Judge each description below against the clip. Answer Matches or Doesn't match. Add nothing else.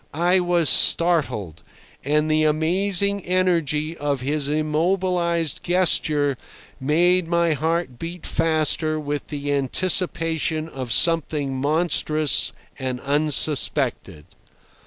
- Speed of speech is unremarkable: Doesn't match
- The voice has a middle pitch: Matches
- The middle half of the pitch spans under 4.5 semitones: Matches